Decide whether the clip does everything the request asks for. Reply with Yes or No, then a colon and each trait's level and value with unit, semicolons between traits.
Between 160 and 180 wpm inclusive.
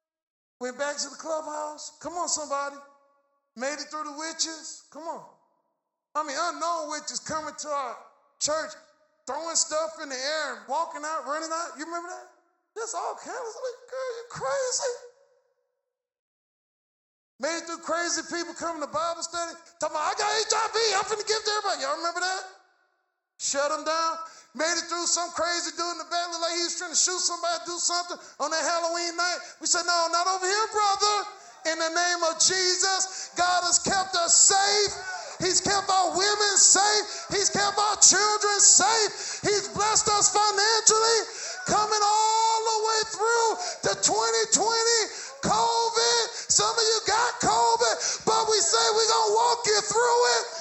Yes: average, 170 wpm